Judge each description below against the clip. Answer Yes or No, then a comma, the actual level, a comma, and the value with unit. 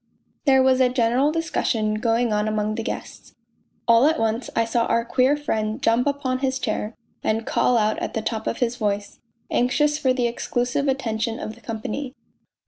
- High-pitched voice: Yes, high, 235 Hz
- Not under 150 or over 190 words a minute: Yes, average, 185 wpm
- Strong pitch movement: No, average, 2.9 semitones